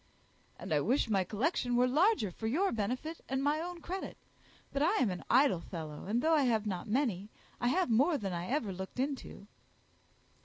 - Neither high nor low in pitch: No, high, 245 Hz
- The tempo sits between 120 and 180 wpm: No, average, 195 wpm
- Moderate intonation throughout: No, wide, 6.8 semitones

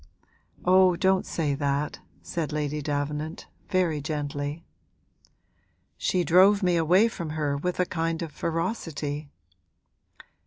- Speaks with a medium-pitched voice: Yes, medium, 160 Hz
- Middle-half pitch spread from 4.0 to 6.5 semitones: No, average, 3.5 semitones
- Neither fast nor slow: No, slow, 115 wpm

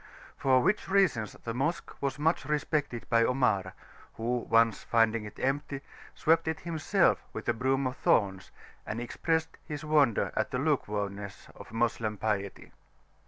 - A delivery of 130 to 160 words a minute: Yes, average, 150 wpm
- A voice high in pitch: No, low, 125 Hz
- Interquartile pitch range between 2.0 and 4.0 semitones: No, average, 5.3 semitones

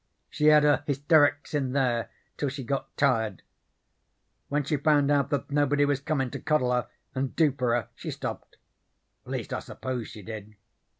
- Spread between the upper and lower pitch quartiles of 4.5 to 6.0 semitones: No, average, 2.8 semitones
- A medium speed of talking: Yes, average, 180 wpm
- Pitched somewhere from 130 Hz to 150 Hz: Yes, medium, 140 Hz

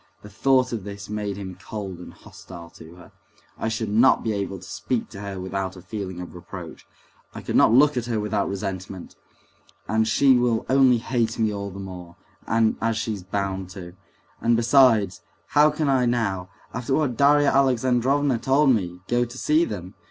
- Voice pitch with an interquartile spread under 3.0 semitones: No, average, 4.5 semitones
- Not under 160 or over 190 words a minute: Yes, average, 185 wpm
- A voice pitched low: Yes, low, 110 Hz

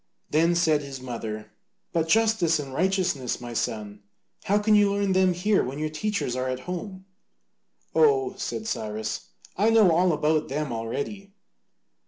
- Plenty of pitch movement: Yes, wide, 7.5 semitones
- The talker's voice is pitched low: No, medium, 165 Hz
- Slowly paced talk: No, average, 155 wpm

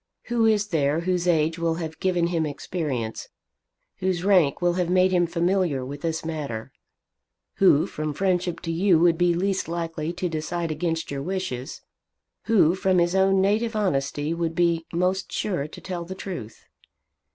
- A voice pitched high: No, medium, 170 Hz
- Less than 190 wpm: Yes, average, 165 wpm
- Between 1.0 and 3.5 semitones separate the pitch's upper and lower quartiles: Yes, average, 2.8 semitones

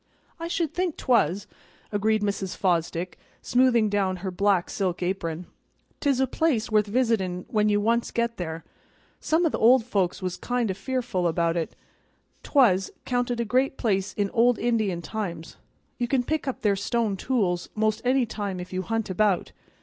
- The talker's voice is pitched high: Yes, high, 210 Hz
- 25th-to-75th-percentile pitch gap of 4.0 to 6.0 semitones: Yes, average, 4.7 semitones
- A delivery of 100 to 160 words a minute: No, average, 175 wpm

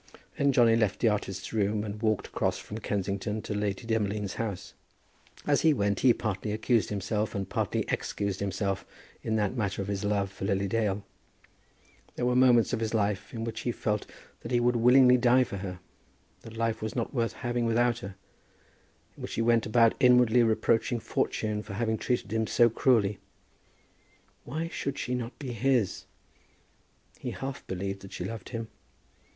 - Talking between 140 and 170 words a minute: No, average, 180 wpm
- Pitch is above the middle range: No, low, 110 Hz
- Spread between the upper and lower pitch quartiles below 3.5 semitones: Yes, average, 3.1 semitones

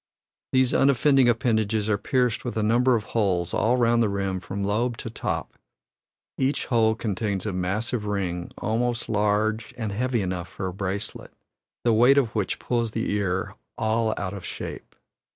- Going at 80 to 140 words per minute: No, average, 170 wpm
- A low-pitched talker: Yes, low, 110 Hz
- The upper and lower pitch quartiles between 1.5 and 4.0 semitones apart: Yes, average, 3.1 semitones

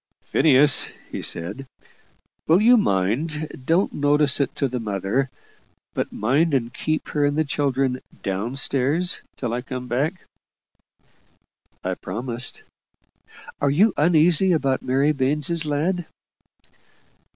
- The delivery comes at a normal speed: No, slow, 120 wpm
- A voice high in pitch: No, medium, 140 Hz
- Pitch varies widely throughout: No, average, 3.7 semitones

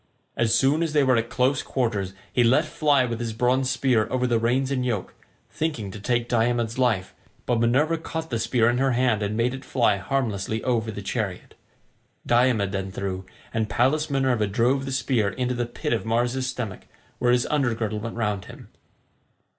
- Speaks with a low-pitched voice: Yes, low, 120 Hz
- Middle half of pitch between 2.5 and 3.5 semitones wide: Yes, average, 2.8 semitones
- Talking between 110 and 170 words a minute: No, average, 195 wpm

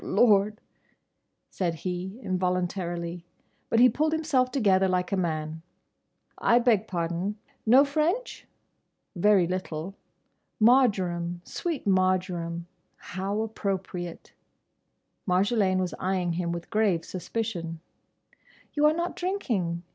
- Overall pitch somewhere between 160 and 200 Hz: Yes, high, 190 Hz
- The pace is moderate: No, slow, 100 wpm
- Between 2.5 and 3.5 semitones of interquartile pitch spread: No, average, 4.5 semitones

